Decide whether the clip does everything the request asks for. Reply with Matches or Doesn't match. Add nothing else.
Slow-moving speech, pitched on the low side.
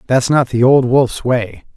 Doesn't match